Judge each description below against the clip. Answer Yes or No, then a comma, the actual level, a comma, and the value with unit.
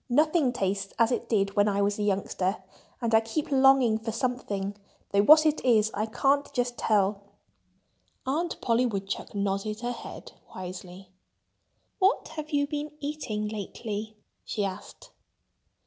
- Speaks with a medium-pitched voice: No, high, 220 Hz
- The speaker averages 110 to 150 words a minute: Yes, average, 145 wpm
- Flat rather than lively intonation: No, average, 5.0 semitones